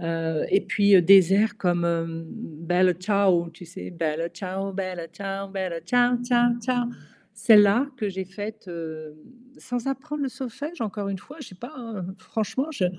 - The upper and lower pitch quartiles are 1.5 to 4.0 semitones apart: No, wide, 5.4 semitones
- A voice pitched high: Yes, high, 195 Hz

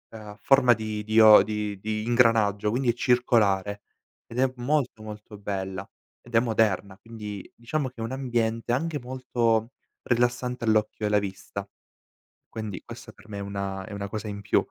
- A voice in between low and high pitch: No, low, 110 Hz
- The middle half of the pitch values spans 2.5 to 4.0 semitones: Yes, average, 2.8 semitones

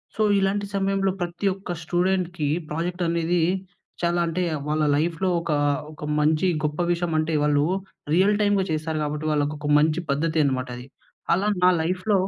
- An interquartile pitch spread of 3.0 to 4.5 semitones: Yes, average, 3.3 semitones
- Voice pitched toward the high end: No, medium, 170 Hz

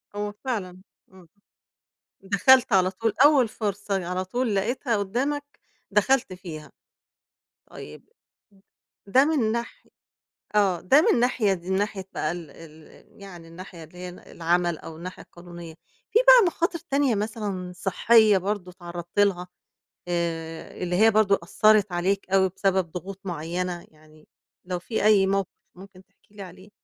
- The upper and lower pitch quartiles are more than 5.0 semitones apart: No, average, 3.4 semitones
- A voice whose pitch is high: Yes, high, 195 Hz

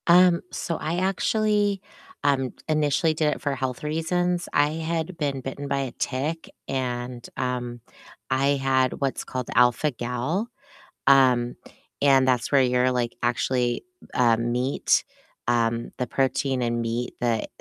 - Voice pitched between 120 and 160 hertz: Yes, low, 135 Hz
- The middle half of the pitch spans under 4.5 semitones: Yes, average, 4.0 semitones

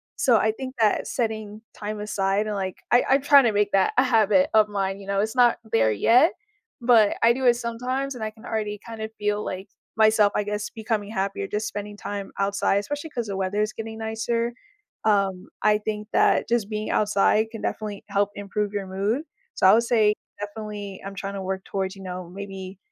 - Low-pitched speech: No, high, 210 Hz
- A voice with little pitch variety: Yes, narrow, 2.1 semitones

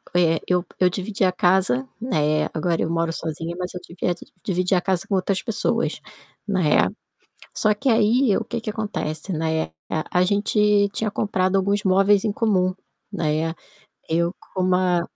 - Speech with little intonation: No, average, 3.3 semitones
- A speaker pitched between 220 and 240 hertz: No, medium, 185 Hz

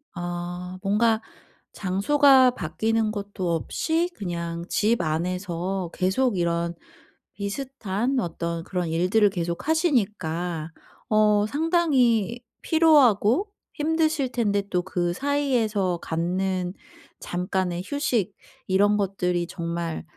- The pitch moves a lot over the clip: Yes, wide, 5.7 semitones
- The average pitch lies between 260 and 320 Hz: No, high, 195 Hz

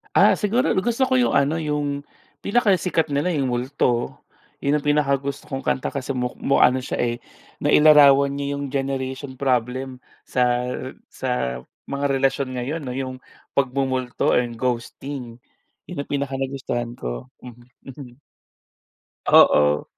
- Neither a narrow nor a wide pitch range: No, narrow, 2.3 semitones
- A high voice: No, low, 135 Hz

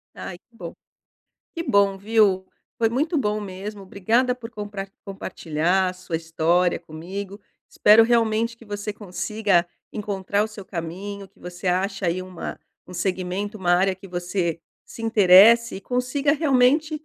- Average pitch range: Yes, average, 3.6 semitones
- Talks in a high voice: Yes, high, 200 Hz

